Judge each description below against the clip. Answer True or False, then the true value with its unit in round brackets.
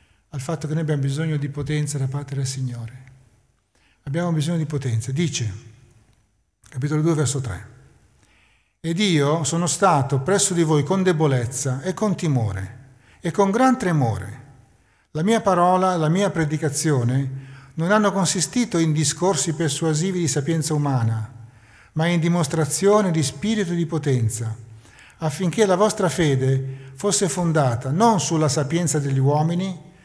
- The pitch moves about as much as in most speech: True (5.0 semitones)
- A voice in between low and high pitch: True (150 Hz)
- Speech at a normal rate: True (140 wpm)